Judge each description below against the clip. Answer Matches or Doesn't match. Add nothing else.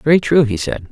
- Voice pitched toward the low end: Matches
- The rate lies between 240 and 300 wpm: Matches